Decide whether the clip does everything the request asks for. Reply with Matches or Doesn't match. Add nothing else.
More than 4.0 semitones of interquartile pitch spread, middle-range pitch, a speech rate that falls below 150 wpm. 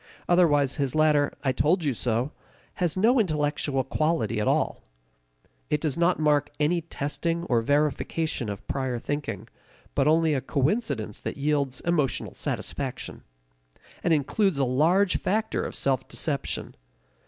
Doesn't match